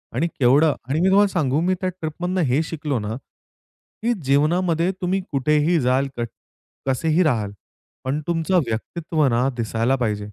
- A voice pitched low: No, medium, 150 Hz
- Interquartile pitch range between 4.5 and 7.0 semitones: Yes, average, 5.1 semitones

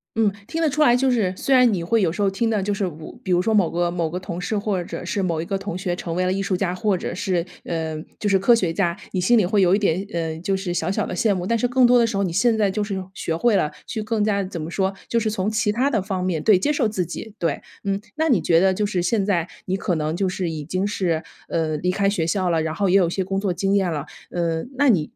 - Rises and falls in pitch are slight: No, average, 3.4 semitones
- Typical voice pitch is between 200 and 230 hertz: No, high, 190 Hz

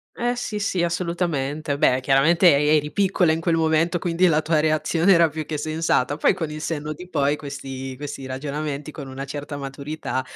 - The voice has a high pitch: No, medium, 155 Hz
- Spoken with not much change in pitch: No, average, 3.0 semitones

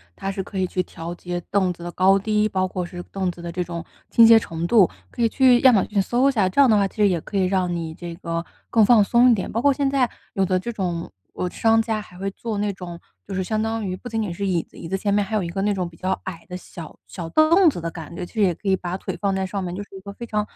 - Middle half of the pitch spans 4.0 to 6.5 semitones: No, average, 3.6 semitones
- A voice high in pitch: Yes, high, 195 Hz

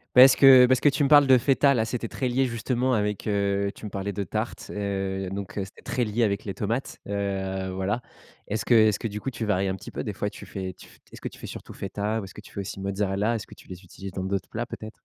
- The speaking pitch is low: Yes, low, 105 Hz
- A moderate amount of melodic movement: Yes, average, 3.5 semitones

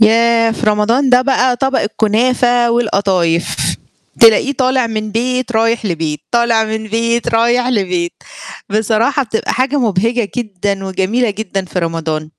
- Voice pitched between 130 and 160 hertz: No, high, 225 Hz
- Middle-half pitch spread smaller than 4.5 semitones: Yes, average, 3.4 semitones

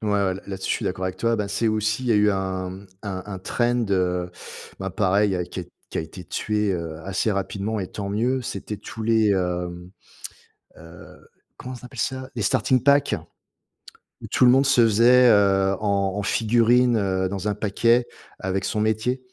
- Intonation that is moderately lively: Yes, average, 3.5 semitones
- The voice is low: Yes, low, 100 Hz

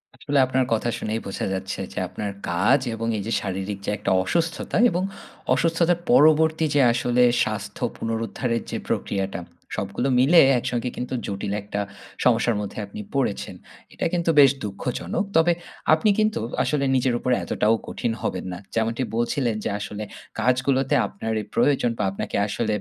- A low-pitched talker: Yes, low, 120 Hz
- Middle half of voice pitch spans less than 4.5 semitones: No, average, 5.0 semitones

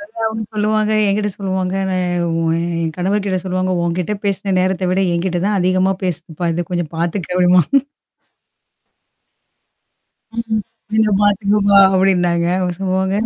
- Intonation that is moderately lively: No, narrow, 2.3 semitones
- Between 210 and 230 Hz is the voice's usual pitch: No, high, 190 Hz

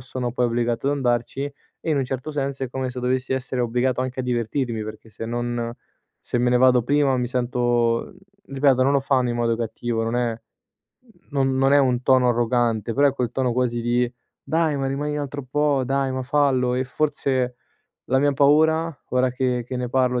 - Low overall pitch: Yes, low, 125 Hz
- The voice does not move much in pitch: Yes, narrow, 2.1 semitones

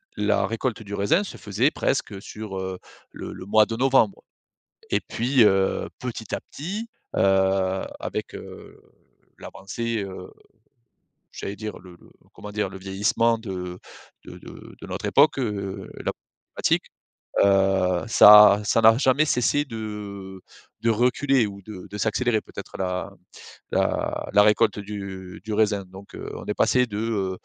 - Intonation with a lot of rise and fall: No, average, 3.0 semitones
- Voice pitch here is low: Yes, low, 105 Hz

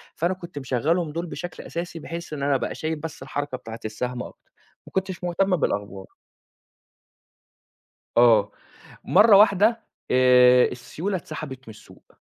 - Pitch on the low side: No, medium, 150 Hz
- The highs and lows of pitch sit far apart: Yes, wide, 6.0 semitones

